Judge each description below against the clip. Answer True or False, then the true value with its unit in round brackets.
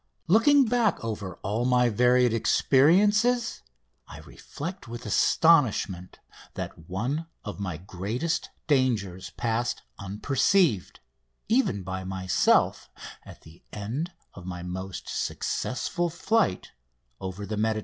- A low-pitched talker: True (115 Hz)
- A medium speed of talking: False (110 wpm)